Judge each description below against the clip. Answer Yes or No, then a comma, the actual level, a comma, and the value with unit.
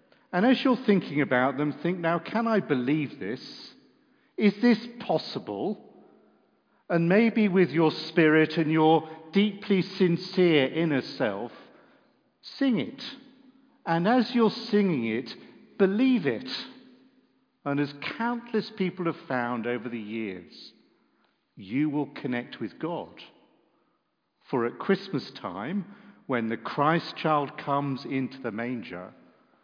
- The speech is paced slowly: Yes, slow, 125 wpm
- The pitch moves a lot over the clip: Yes, wide, 7.8 semitones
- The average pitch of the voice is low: No, medium, 170 Hz